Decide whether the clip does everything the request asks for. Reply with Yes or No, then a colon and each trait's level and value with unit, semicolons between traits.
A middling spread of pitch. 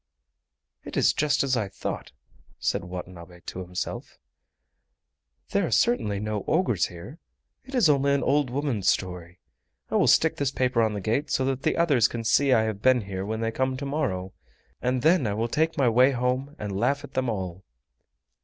No: wide, 5.9 semitones